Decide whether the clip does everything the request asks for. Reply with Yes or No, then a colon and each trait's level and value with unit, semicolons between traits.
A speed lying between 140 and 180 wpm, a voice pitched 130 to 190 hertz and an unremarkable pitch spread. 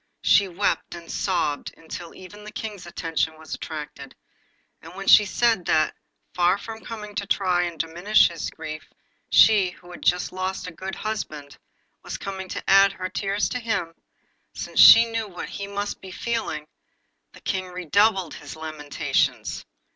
Yes: average, 160 wpm; medium, 185 Hz; average, 3.5 semitones